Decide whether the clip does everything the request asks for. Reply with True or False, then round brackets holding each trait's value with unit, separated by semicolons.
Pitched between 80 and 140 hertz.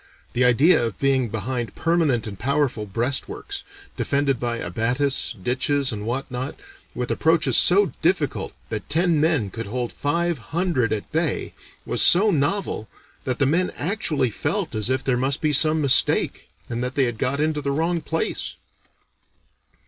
True (135 Hz)